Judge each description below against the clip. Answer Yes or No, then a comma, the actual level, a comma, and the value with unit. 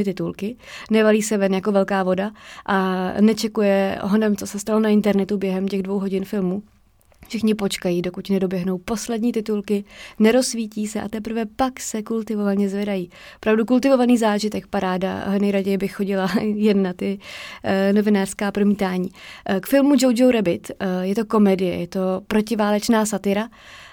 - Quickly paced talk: No, average, 150 wpm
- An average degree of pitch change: No, narrow, 2.1 semitones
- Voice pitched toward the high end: Yes, high, 205 Hz